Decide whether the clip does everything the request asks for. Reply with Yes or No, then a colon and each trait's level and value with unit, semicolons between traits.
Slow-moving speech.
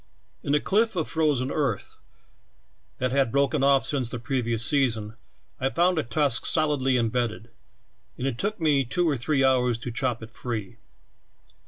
No: average, 175 wpm